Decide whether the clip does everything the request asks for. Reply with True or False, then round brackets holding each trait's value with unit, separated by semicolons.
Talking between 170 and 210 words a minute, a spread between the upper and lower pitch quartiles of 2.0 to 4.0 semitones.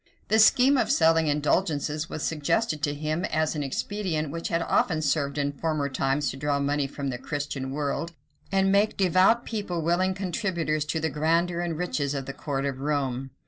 True (185 wpm; 3.6 semitones)